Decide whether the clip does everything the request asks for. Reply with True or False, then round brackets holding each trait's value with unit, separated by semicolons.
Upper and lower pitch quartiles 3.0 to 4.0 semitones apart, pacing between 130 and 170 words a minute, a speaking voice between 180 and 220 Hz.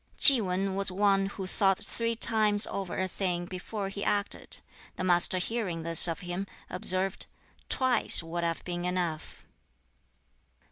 False (2.4 semitones; 145 wpm; 190 Hz)